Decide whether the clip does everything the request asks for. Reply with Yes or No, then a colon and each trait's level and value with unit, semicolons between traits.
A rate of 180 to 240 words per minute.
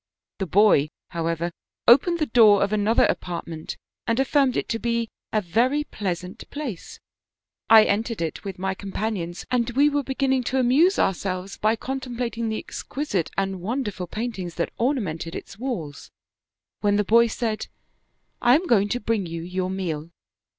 No: average, 165 wpm